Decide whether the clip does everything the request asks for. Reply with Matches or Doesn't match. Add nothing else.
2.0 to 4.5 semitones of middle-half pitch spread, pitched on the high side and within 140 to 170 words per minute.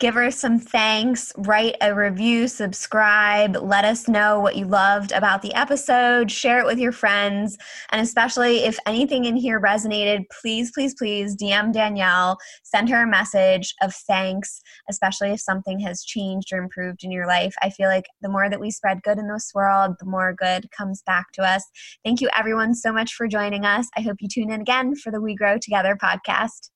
Doesn't match